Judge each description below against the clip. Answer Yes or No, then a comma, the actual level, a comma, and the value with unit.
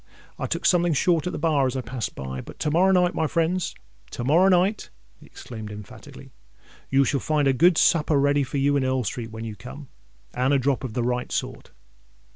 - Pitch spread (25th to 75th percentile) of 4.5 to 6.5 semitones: Yes, average, 4.8 semitones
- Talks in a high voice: No, medium, 140 Hz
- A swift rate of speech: Yes, fast, 215 wpm